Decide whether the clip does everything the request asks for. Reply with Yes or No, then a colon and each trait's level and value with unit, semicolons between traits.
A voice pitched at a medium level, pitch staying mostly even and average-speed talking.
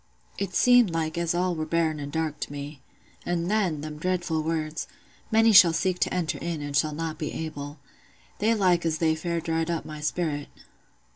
Yes: medium, 165 Hz; narrow, 2.3 semitones; average, 195 wpm